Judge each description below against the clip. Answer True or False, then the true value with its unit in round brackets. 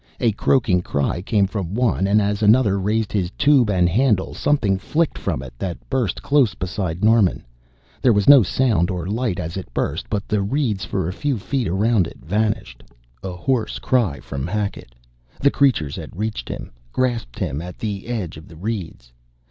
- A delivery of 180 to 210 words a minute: True (185 wpm)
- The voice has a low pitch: True (100 Hz)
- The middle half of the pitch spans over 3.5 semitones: True (4.6 semitones)